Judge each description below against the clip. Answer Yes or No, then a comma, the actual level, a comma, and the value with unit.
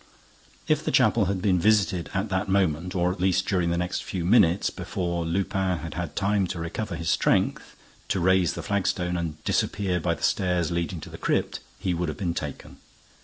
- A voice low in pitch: Yes, very low, 90 Hz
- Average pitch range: No, narrow, 2.1 semitones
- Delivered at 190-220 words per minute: Yes, average, 200 wpm